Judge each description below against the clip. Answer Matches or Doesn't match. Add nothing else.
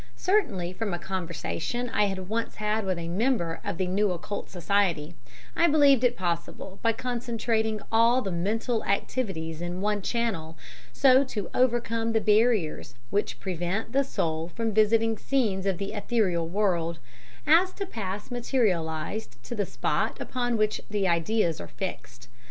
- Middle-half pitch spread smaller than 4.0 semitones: Doesn't match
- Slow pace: Doesn't match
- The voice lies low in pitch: Doesn't match